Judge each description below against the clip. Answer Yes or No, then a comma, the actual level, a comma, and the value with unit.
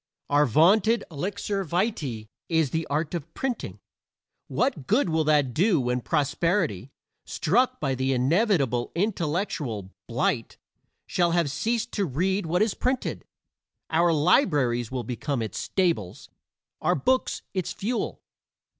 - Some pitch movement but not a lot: No, wide, 6.7 semitones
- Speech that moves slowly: Yes, slow, 130 wpm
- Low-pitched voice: No, medium, 160 Hz